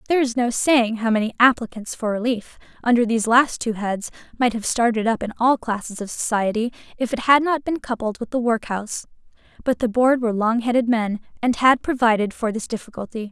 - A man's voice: No, female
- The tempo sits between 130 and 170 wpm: No, fast, 205 wpm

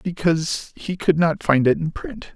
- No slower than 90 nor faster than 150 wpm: No, fast, 205 wpm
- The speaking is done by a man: Yes, male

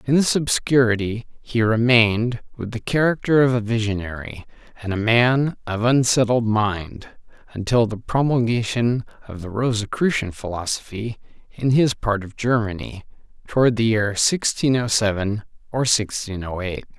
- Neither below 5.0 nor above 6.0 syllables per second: No, 4.6 syllables/s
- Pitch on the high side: No, low, 115 Hz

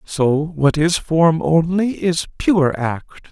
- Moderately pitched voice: Yes, medium, 160 Hz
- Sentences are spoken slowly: No, average, 145 wpm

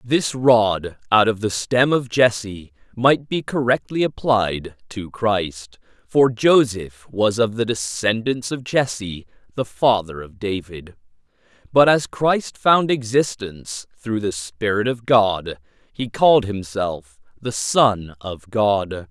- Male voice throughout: Yes, male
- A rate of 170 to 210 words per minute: No, slow, 135 wpm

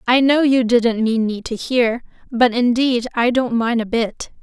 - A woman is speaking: Yes, female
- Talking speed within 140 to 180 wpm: No, fast, 205 wpm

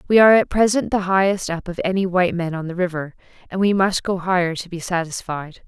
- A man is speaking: No, female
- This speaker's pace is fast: Yes, fast, 235 wpm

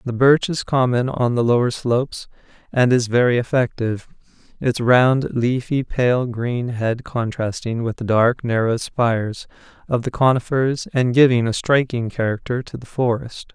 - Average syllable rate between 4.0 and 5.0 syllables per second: Yes, 4.5 syllables/s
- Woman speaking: No, male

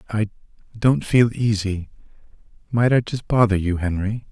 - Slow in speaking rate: Yes, slow, 125 wpm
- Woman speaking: No, male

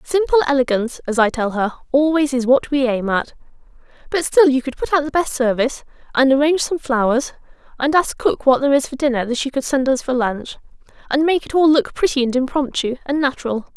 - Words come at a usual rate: No, fast, 220 wpm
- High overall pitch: Yes, very high, 275 Hz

